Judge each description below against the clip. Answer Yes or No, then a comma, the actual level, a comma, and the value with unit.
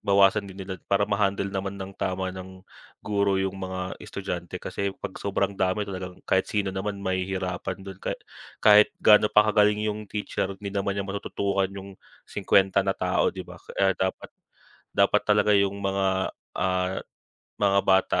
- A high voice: No, very low, 95 Hz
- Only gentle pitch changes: Yes, narrow, 1.0 semitones